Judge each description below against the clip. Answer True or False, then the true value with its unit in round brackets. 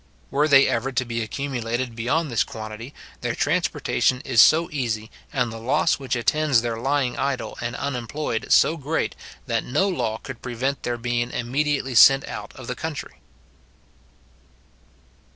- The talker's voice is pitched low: True (125 Hz)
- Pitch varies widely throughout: False (3.1 semitones)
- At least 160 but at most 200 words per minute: False (150 wpm)